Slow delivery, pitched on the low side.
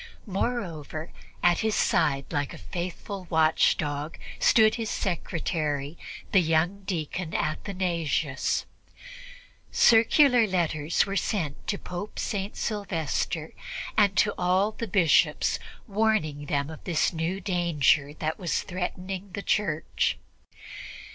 No: slow, 110 wpm; medium, 175 Hz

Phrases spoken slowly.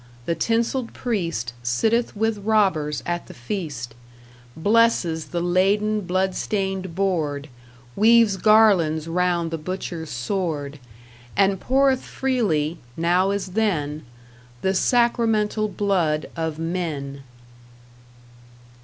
Yes: slow, 100 wpm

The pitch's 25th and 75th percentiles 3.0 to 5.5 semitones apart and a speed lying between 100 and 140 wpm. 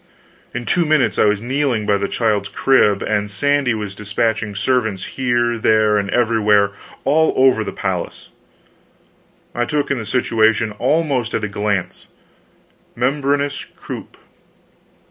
Yes: average, 4.2 semitones; slow, 135 wpm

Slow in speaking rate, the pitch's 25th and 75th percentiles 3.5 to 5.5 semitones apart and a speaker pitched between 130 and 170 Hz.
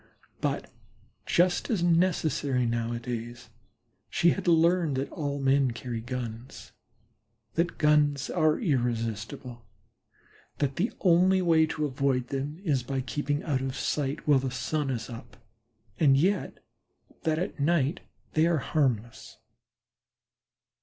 Yes: slow, 125 wpm; average, 4.3 semitones; medium, 140 Hz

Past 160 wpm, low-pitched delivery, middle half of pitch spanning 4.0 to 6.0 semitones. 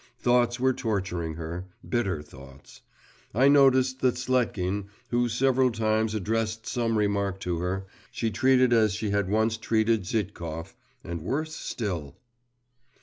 No: slow, 135 wpm; low, 110 Hz; average, 4.6 semitones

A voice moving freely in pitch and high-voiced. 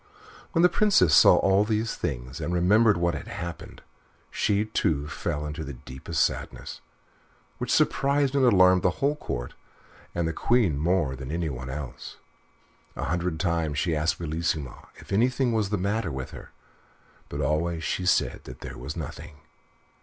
No: wide, 5.8 semitones; very low, 85 Hz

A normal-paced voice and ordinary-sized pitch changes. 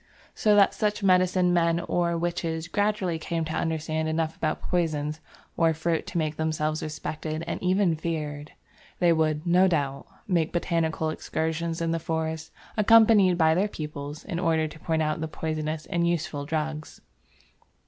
No: average, 160 wpm; narrow, 1.8 semitones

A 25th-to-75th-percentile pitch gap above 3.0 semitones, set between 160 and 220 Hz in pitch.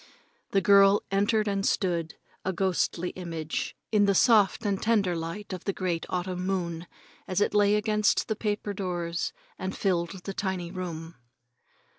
No: average, 2.7 semitones; high, 190 Hz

